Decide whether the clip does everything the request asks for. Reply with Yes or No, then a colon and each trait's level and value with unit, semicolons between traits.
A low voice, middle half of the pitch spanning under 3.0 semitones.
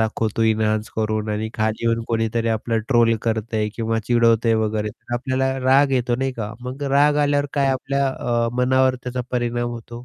Yes: low, 115 Hz; narrow, 2.6 semitones